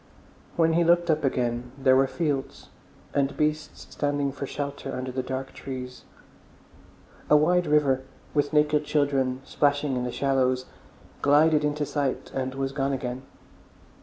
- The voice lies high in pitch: No, medium, 140 Hz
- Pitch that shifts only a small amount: Yes, narrow, 2.3 semitones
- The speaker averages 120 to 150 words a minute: Yes, average, 145 wpm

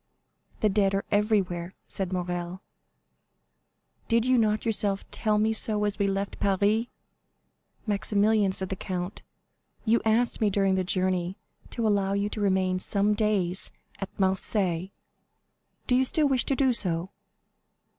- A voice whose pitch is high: Yes, high, 200 Hz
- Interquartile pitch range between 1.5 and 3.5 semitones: Yes, narrow, 2.4 semitones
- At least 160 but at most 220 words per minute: No, average, 145 wpm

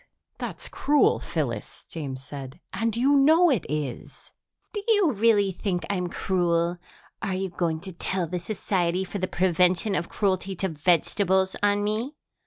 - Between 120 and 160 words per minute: Yes, average, 155 wpm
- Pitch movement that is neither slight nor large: Yes, average, 3.6 semitones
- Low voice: No, high, 190 Hz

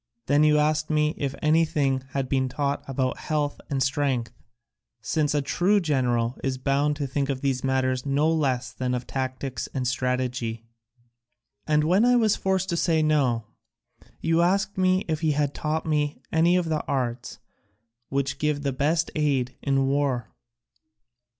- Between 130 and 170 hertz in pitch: Yes, medium, 140 Hz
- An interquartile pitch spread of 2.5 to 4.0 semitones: Yes, average, 3.0 semitones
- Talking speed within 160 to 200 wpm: Yes, average, 165 wpm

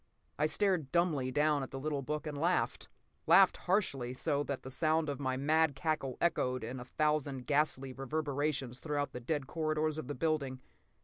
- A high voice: No, medium, 145 Hz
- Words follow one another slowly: No, average, 180 wpm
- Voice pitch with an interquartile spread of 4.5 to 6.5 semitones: No, average, 2.8 semitones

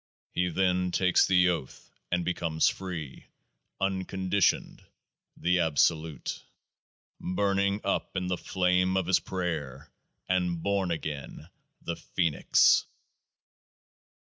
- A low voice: Yes, very low, 90 Hz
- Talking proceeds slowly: Yes, slow, 115 wpm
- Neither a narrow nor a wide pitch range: No, narrow, 2.2 semitones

